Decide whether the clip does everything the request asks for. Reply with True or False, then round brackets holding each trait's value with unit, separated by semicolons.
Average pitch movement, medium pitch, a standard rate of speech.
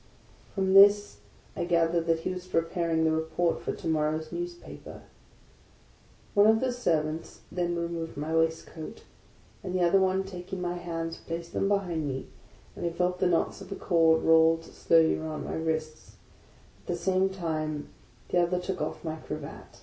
False (2.3 semitones; 170 Hz; 175 wpm)